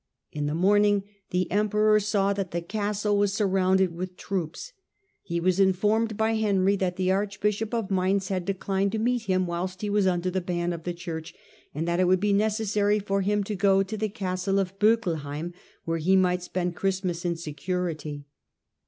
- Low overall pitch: No, high, 190 Hz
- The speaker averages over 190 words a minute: Yes, average, 200 wpm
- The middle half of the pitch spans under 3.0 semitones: Yes, narrow, 2.5 semitones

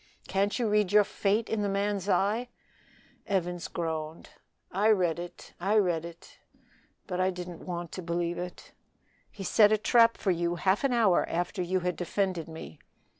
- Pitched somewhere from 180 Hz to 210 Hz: Yes, medium, 185 Hz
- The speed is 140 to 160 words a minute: No, average, 175 wpm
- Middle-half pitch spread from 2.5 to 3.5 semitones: Yes, average, 3.1 semitones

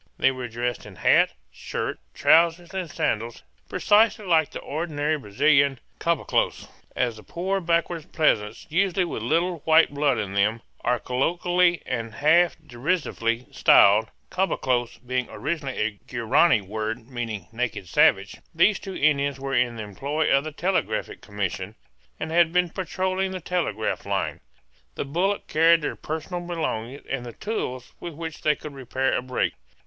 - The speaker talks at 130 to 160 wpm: Yes, average, 155 wpm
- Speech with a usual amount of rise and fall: No, wide, 6.4 semitones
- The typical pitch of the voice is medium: Yes, medium, 145 Hz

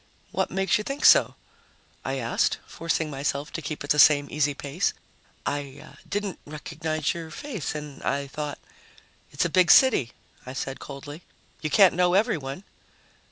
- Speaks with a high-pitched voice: No, medium, 150 Hz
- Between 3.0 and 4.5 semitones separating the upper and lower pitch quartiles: Yes, average, 3.9 semitones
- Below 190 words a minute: Yes, average, 160 wpm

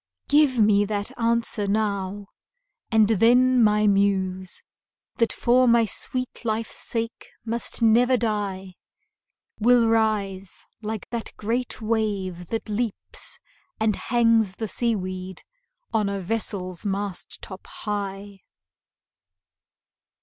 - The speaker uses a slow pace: Yes, slow, 110 wpm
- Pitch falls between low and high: No, high, 215 Hz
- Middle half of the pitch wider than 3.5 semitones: No, narrow, 2.6 semitones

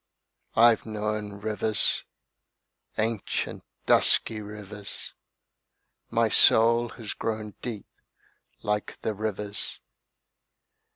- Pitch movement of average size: No, narrow, 1.1 semitones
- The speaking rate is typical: No, slow, 75 wpm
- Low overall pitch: Yes, low, 105 Hz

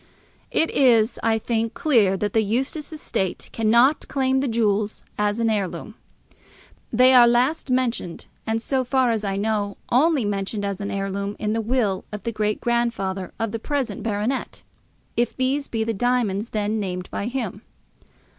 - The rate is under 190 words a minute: Yes, average, 165 wpm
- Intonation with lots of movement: No, average, 3.6 semitones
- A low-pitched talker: No, high, 225 Hz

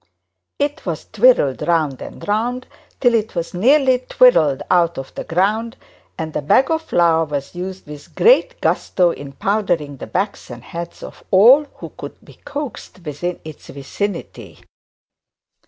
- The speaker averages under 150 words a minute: No, average, 155 wpm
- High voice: No, medium, 180 Hz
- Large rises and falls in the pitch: Yes, wide, 7.6 semitones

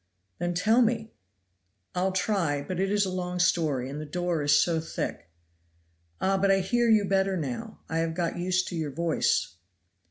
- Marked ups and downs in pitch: No, average, 3.2 semitones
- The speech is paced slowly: No, average, 185 wpm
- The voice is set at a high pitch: No, medium, 180 Hz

